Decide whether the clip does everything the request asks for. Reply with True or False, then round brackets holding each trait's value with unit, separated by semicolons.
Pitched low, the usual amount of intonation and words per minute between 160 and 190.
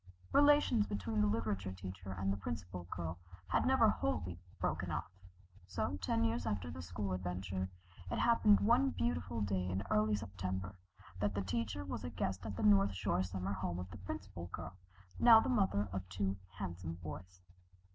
False (95 Hz; 2.3 semitones; 175 wpm)